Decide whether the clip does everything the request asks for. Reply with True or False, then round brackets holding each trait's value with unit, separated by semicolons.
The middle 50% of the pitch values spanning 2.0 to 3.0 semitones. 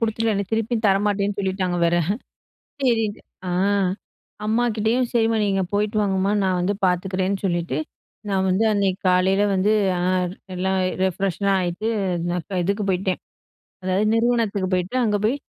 True (2.7 semitones)